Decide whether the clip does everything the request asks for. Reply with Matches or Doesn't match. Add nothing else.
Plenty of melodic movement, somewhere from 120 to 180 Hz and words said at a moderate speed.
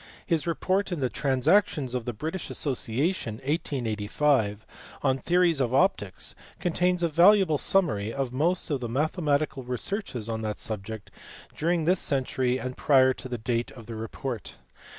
Matches